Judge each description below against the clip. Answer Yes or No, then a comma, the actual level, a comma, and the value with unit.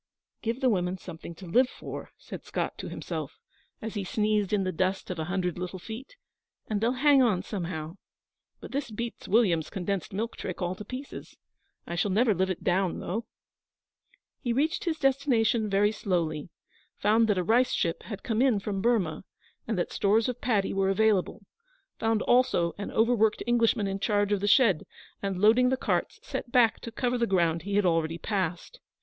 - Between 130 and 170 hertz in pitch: No, high, 205 Hz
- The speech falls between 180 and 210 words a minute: Yes, average, 190 wpm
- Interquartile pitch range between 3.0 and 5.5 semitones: Yes, average, 4.1 semitones